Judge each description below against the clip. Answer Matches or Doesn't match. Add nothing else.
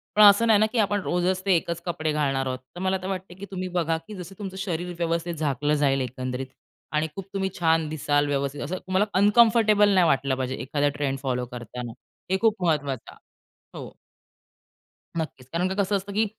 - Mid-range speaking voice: Matches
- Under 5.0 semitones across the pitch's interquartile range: Doesn't match